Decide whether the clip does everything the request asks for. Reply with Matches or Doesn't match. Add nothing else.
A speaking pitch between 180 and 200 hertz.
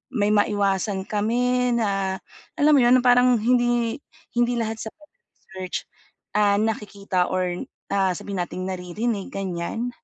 Doesn't match